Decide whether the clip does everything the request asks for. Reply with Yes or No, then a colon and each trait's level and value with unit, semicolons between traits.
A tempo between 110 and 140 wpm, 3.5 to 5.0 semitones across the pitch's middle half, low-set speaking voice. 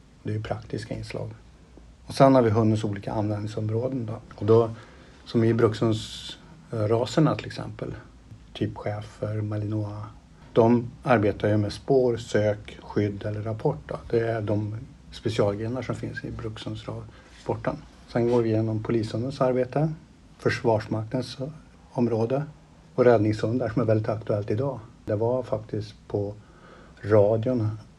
No: average, 130 wpm; average, 2.8 semitones; low, 115 Hz